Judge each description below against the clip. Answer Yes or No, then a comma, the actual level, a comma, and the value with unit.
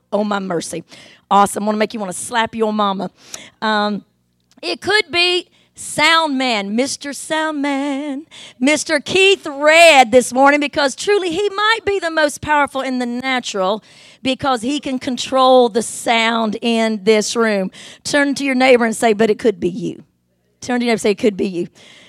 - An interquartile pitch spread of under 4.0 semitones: No, average, 5.3 semitones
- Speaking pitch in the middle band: No, very high, 250 Hz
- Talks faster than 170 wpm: Yes, average, 185 wpm